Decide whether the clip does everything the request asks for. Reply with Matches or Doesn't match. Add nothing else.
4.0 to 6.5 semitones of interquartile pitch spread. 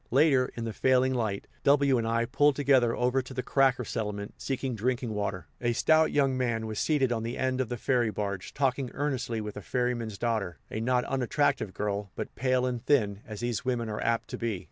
Doesn't match